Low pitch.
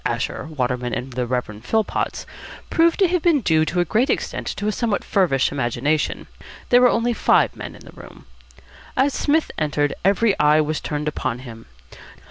No: medium, 155 Hz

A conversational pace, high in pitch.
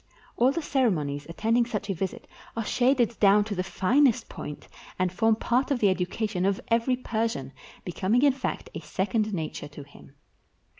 Yes: average, 170 wpm; high, 215 Hz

